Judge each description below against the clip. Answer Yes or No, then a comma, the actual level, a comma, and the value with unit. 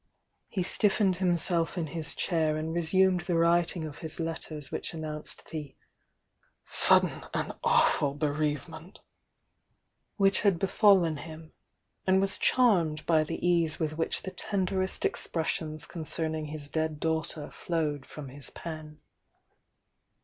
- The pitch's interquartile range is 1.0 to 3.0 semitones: Yes, narrow, 2.5 semitones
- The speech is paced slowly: Yes, slow, 130 wpm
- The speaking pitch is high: No, medium, 160 Hz